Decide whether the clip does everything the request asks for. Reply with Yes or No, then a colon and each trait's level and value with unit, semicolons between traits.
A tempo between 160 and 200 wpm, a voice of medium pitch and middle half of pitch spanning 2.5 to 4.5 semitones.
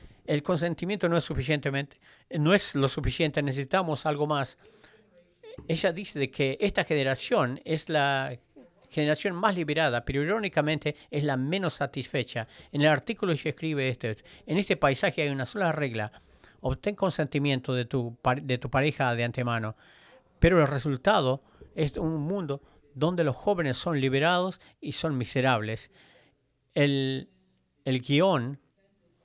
No: average, 140 wpm; medium, 145 Hz; average, 4.1 semitones